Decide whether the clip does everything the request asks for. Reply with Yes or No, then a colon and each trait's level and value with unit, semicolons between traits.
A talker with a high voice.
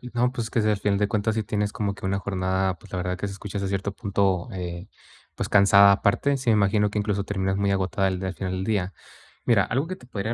No: low, 100 Hz